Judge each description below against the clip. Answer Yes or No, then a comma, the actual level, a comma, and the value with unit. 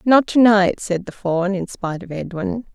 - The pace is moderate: No, fast, 220 wpm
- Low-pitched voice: No, high, 195 Hz